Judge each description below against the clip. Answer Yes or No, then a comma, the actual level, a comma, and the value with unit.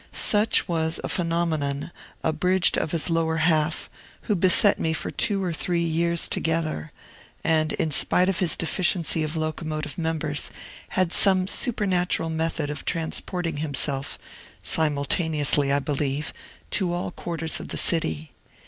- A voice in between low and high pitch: Yes, medium, 160 Hz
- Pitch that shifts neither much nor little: No, narrow, 2.3 semitones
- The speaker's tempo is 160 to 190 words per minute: No, average, 140 wpm